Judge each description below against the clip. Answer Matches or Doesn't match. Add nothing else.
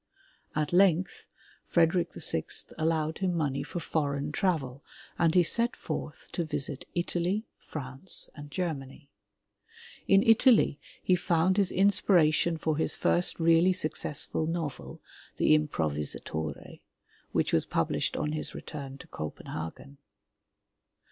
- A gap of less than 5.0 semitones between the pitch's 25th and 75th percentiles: Matches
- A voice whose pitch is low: Doesn't match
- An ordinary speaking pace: Doesn't match